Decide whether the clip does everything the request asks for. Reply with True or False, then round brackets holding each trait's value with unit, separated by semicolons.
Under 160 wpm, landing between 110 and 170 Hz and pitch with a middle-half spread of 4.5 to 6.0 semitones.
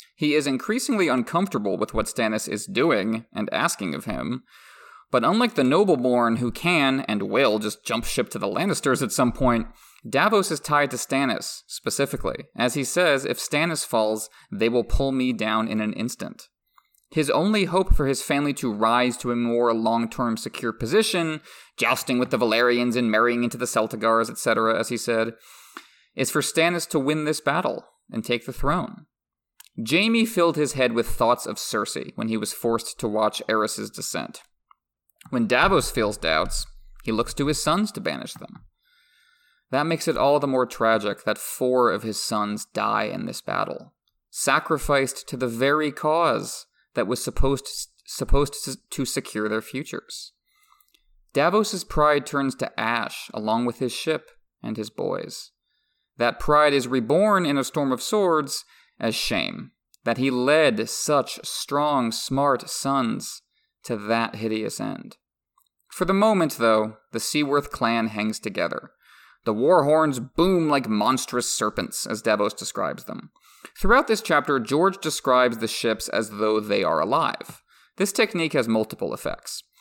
False (165 wpm; 135 Hz; 5.1 semitones)